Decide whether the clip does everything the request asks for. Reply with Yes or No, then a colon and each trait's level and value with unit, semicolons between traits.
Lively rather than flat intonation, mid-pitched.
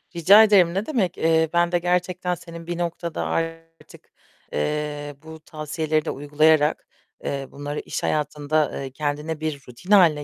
No: narrow, 2.6 semitones; medium, 160 Hz